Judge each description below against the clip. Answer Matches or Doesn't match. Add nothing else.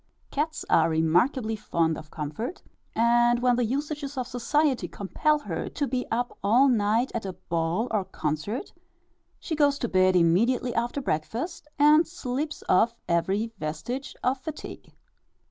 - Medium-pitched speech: Doesn't match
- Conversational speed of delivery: Matches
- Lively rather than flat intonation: Matches